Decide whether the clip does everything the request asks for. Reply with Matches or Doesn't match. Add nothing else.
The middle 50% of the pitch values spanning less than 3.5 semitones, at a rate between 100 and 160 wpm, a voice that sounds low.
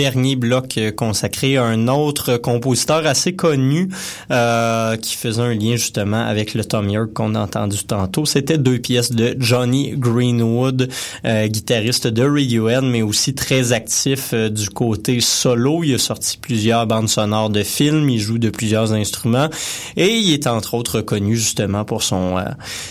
Doesn't match